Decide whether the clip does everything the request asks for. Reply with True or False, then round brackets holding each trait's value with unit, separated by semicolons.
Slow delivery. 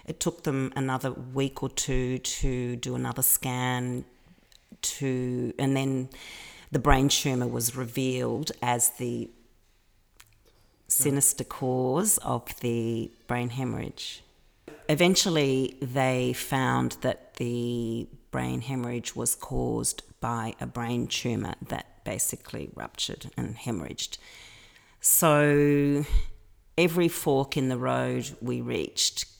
True (110 wpm)